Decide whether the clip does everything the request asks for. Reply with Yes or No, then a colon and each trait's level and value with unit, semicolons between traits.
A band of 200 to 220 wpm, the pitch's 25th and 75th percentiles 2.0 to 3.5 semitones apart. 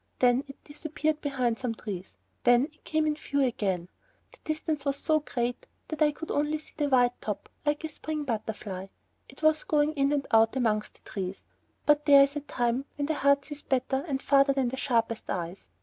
No: fast, 205 wpm; average, 3.9 semitones